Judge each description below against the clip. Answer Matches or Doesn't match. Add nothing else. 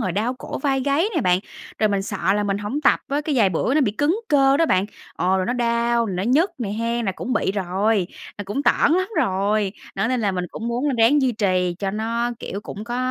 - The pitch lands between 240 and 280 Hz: Doesn't match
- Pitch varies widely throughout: Doesn't match